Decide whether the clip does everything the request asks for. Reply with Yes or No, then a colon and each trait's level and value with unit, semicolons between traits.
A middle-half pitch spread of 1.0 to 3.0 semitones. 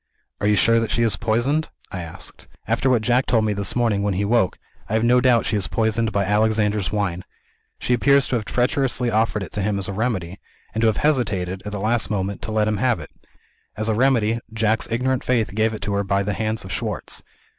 Yes: narrow, 2.6 semitones